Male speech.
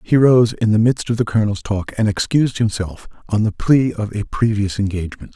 Yes: male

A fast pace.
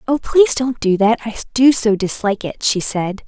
Yes: fast, 220 wpm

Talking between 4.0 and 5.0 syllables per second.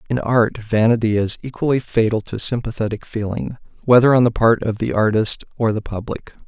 No: 5.4 syllables/s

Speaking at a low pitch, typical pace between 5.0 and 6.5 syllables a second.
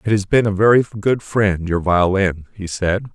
No: low, 100 Hz; 4.5 syllables/s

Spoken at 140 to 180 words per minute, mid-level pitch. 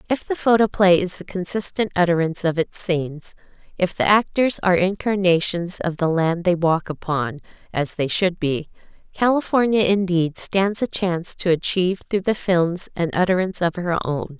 Yes: average, 165 wpm; medium, 180 Hz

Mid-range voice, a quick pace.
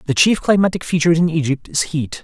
Yes: medium, 160 Hz; fast, 215 wpm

